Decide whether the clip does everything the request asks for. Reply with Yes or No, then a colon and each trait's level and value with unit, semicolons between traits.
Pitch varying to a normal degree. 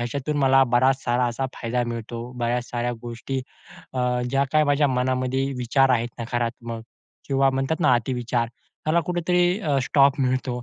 No: narrow, 2.2 semitones